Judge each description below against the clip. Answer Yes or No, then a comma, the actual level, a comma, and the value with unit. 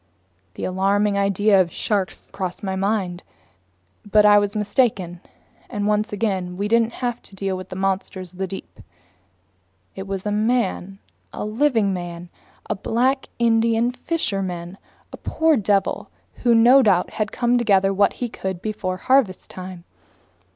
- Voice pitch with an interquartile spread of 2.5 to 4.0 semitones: Yes, average, 3.1 semitones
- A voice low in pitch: No, high, 200 Hz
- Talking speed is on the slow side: No, average, 150 wpm